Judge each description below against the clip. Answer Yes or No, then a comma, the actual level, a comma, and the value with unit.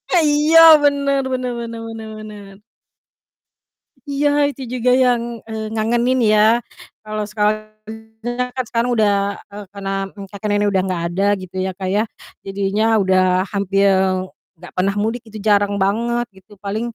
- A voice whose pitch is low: No, high, 215 Hz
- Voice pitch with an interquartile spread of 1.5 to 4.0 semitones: Yes, average, 3.2 semitones